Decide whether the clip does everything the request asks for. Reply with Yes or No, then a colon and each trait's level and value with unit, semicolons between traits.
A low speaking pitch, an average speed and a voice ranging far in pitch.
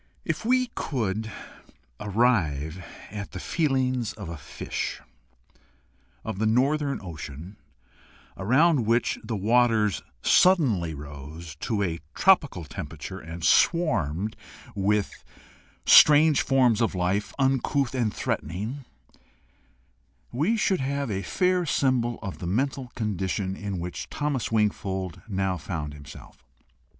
No: low, 105 Hz; slow, 110 wpm; wide, 6.7 semitones